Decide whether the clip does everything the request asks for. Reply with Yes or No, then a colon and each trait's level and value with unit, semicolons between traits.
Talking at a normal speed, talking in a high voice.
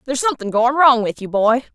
No: fast, 240 wpm; high, 245 Hz